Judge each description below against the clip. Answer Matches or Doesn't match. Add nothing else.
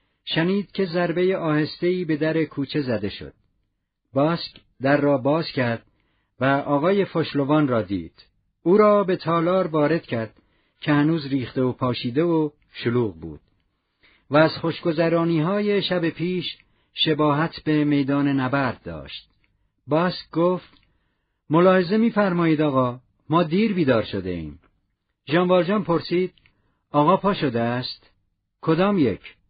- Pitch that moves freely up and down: Matches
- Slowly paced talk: Matches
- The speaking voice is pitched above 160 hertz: Doesn't match